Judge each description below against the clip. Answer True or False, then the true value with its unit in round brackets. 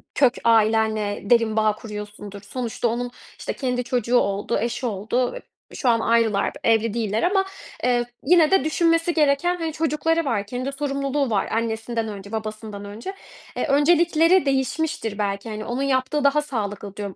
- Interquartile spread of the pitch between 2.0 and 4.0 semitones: False (4.9 semitones)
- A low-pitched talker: False (240 Hz)